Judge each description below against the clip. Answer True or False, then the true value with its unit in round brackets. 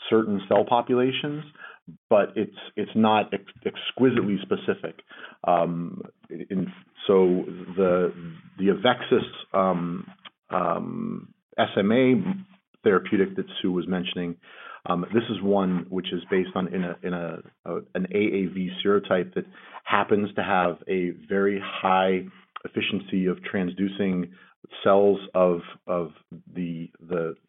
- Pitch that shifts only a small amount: True (2.2 semitones)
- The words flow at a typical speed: False (120 wpm)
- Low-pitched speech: True (95 Hz)